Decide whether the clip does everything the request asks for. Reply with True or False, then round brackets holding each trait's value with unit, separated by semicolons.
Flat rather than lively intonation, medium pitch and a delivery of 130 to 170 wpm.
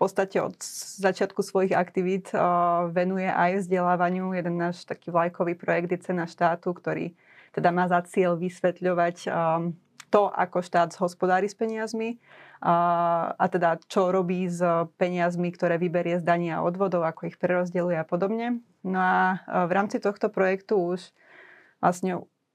True (1.7 semitones; 180 Hz; 155 wpm)